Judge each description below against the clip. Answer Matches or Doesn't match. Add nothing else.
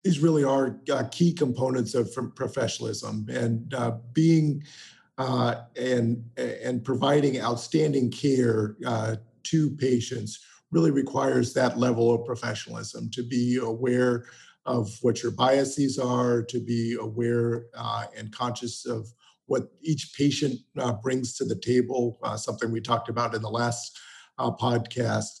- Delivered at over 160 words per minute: Doesn't match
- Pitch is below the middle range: Matches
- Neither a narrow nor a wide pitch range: Doesn't match